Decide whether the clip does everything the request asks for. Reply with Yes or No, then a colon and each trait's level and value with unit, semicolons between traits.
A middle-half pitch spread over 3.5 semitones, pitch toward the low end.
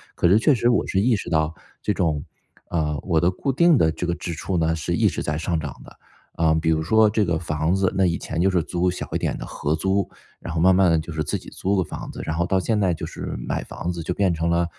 No: average, 3.2 semitones; very low, 85 Hz